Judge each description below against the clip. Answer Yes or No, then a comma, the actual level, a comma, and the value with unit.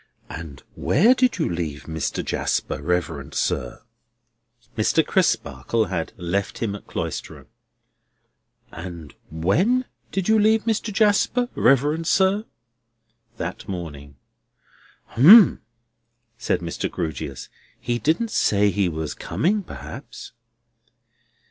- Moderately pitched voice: No, low, 110 Hz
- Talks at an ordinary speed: No, slow, 105 wpm